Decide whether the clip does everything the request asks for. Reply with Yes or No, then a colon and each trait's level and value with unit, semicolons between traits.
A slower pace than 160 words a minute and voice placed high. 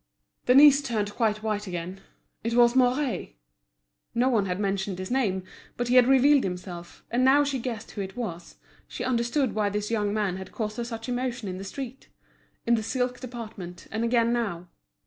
No: average, 185 wpm; high, 230 Hz